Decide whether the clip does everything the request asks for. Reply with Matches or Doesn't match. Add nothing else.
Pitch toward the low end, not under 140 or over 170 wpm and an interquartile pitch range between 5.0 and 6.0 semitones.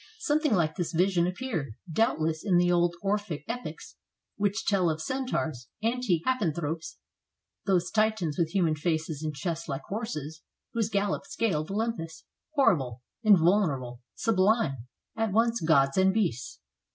Doesn't match